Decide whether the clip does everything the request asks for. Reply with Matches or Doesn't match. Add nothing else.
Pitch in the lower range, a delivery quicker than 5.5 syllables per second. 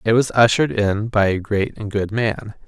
Doesn't match